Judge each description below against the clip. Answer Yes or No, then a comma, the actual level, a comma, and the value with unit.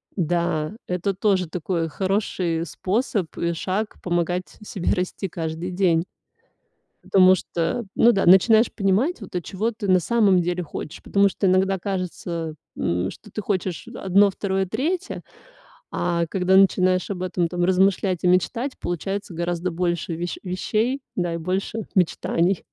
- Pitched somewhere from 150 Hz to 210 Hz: Yes, medium, 185 Hz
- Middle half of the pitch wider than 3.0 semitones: No, narrow, 2.4 semitones